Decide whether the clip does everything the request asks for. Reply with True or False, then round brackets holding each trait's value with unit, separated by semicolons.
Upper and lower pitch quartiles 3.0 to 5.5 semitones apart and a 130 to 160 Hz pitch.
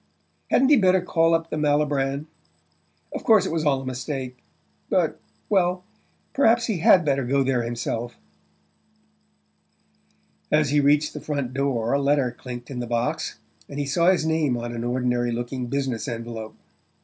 True (4.5 semitones; 140 Hz)